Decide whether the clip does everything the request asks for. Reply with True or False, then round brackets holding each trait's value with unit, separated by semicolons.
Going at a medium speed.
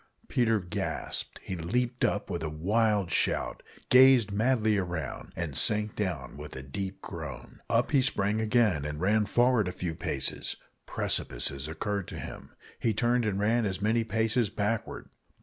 True (160 wpm)